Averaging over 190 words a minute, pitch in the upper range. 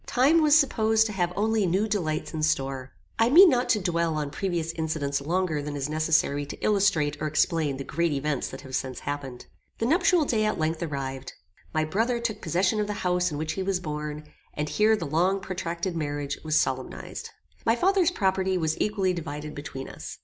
No: average, 200 wpm; medium, 170 Hz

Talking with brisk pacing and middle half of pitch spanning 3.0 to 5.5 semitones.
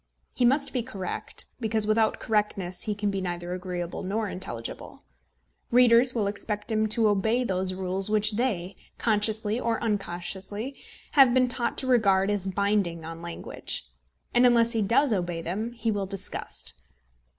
No: average, 155 wpm; average, 3.7 semitones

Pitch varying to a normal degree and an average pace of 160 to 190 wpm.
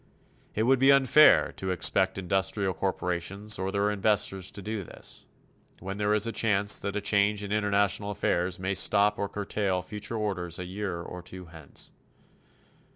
No: narrow, 2.0 semitones; average, 165 wpm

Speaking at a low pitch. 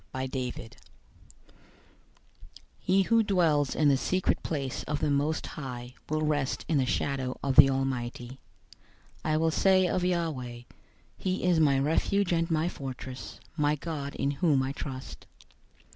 No: medium, 145 Hz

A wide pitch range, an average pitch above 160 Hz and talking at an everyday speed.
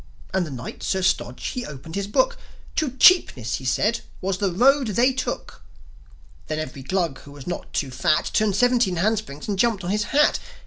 Yes: wide, 7.4 semitones; high, 190 Hz; average, 190 wpm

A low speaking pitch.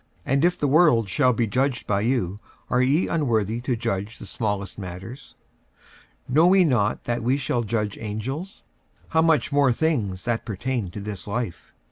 Yes: low, 120 Hz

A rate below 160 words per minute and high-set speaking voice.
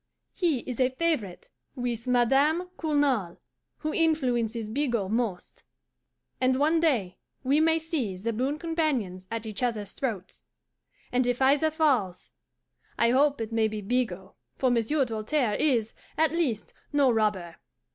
Yes: slow, 135 wpm; very high, 250 Hz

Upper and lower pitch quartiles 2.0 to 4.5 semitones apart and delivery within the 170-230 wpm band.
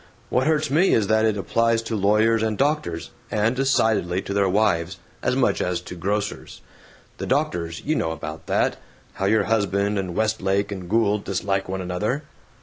Yes: average, 3.2 semitones; average, 175 wpm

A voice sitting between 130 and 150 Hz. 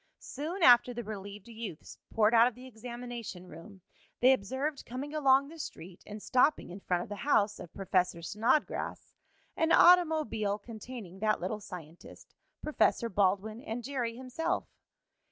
No: high, 230 Hz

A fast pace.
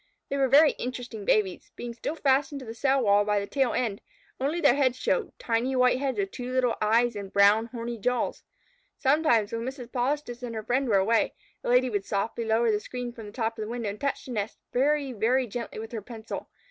Yes: fast, 225 wpm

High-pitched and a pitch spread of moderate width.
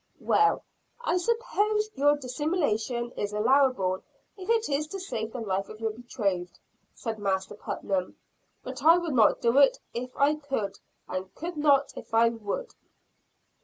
No: very high, 255 Hz; wide, 6.4 semitones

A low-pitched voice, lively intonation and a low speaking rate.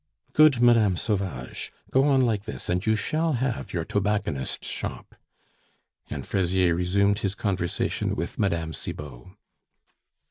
No: low, 100 Hz; average, 4.9 semitones; slow, 130 wpm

